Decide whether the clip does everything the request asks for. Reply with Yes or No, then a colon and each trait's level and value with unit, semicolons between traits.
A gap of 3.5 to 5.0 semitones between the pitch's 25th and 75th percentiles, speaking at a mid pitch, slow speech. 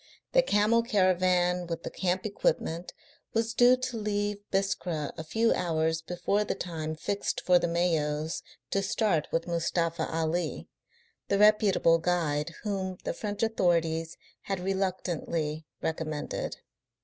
Yes: average, 3.8 semitones; medium, 180 Hz; slow, 130 wpm